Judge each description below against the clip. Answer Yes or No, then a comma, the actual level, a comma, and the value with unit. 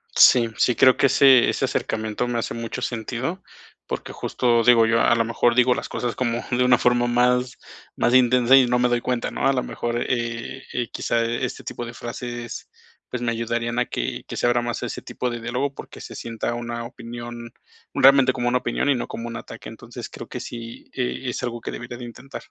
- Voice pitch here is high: No, low, 120 Hz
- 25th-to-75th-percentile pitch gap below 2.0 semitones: Yes, narrow, 1.1 semitones